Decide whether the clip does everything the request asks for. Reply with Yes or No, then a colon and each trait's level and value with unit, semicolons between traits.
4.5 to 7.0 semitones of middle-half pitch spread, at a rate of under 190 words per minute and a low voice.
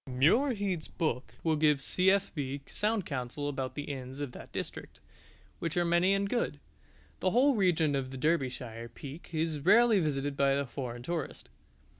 No: average, 5.2 semitones; average, 160 wpm; medium, 150 Hz